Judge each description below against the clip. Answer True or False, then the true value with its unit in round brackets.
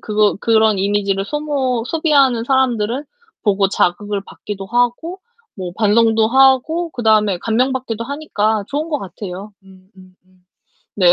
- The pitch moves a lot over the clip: False (4.7 semitones)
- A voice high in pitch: True (220 Hz)